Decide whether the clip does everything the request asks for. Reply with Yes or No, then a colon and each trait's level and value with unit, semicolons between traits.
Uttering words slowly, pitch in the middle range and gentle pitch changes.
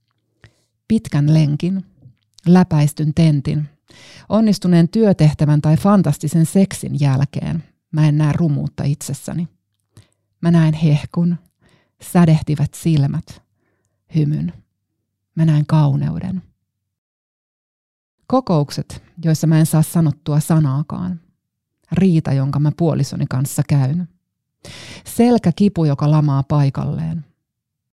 No: slow, 90 wpm; medium, 155 Hz; average, 3.0 semitones